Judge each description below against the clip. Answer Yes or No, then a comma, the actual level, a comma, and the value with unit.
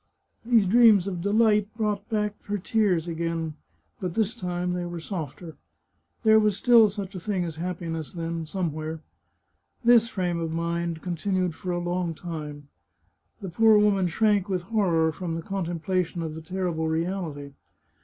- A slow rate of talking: No, average, 160 wpm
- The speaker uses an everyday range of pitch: Yes, average, 3.7 semitones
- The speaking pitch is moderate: Yes, medium, 180 Hz